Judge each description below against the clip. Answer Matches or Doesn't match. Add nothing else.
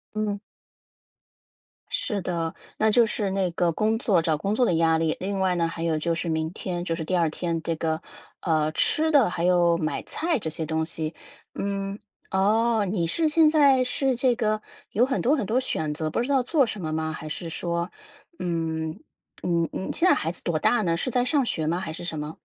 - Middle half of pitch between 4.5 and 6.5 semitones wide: Matches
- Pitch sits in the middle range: Matches